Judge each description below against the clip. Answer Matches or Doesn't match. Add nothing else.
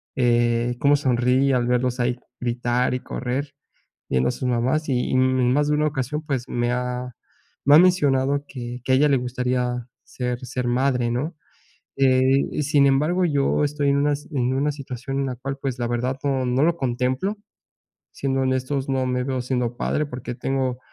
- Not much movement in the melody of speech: Matches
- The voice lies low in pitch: Matches